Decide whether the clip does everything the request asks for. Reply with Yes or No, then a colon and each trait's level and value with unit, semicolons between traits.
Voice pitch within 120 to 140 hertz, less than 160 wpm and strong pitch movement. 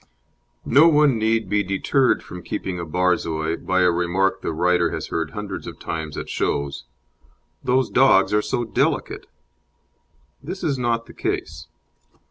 No: very low, 95 Hz; average, 150 wpm; wide, 5.8 semitones